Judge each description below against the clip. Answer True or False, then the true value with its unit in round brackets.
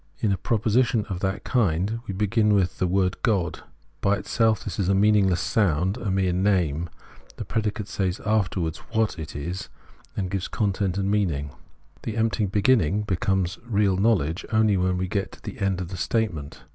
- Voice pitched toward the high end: False (100 Hz)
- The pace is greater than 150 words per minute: True (185 wpm)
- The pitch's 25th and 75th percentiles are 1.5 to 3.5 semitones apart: True (2.7 semitones)